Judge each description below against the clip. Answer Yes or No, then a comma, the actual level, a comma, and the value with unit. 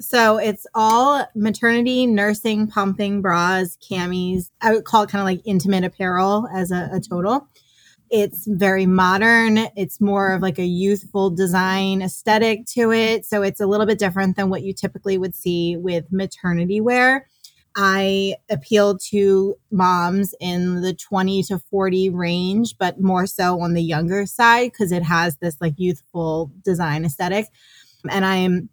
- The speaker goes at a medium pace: Yes, average, 160 wpm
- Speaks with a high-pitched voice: Yes, high, 195 Hz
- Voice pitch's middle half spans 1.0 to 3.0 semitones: Yes, narrow, 2.6 semitones